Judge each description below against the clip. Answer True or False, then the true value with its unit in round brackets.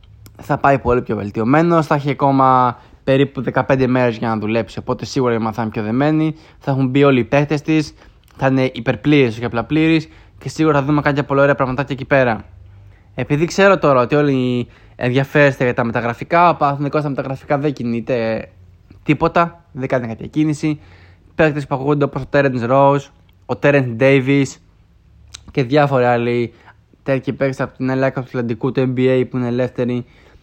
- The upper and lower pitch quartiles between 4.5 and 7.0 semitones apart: False (3.5 semitones)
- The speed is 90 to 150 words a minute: False (170 wpm)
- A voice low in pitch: True (130 Hz)